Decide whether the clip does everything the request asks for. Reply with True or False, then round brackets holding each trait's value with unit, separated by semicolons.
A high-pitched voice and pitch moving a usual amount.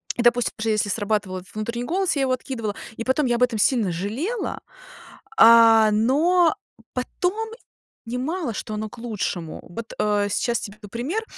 True (230 Hz; 3.7 semitones)